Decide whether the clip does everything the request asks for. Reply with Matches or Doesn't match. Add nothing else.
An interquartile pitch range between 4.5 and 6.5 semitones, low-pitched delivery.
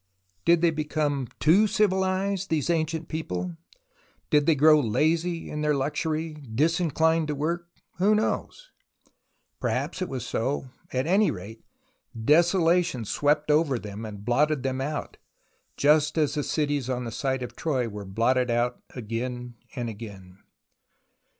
Doesn't match